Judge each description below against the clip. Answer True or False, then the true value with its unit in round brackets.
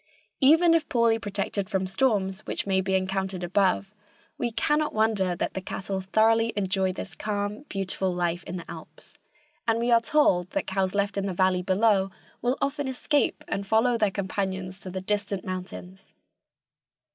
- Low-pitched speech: False (195 Hz)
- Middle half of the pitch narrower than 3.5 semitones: True (3.1 semitones)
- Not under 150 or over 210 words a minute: True (170 wpm)